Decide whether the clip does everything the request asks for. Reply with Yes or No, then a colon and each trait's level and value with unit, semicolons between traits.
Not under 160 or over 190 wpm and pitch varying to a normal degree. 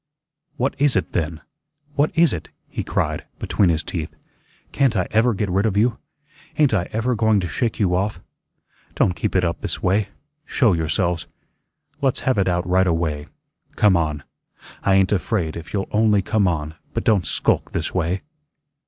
Yes: average, 180 wpm; average, 4.2 semitones